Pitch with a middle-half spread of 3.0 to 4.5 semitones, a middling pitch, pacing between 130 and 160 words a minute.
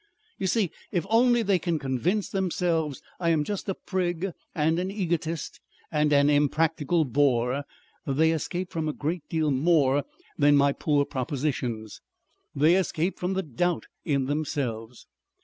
Yes: average, 3.8 semitones; medium, 155 Hz; average, 150 wpm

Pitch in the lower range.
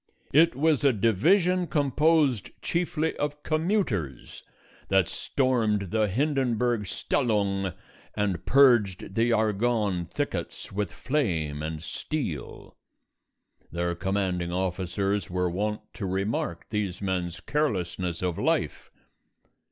Yes: low, 105 Hz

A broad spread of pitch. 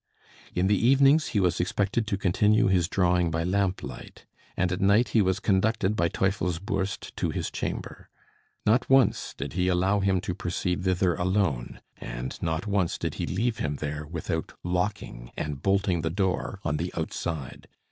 No: average, 3.0 semitones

